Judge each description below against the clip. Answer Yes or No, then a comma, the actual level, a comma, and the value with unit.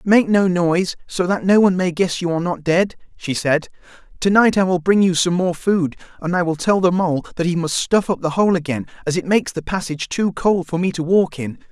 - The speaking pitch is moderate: Yes, medium, 175 Hz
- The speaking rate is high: Yes, fast, 255 wpm